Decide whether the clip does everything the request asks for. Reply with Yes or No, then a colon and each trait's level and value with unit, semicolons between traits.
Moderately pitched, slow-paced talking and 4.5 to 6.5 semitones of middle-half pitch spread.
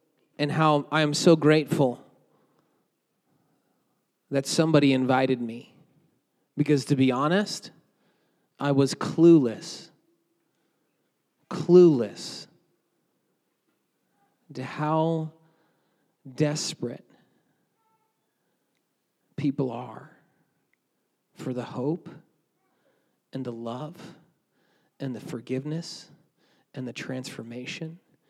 No: medium, 150 Hz; slow, 75 wpm; average, 3.8 semitones